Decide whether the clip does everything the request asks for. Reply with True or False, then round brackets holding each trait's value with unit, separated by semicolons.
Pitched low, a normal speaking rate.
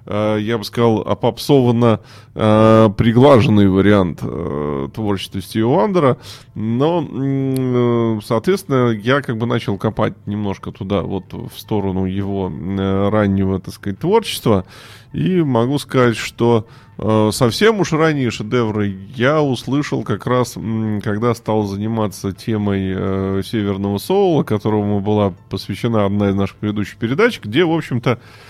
True (110 Hz; 130 wpm)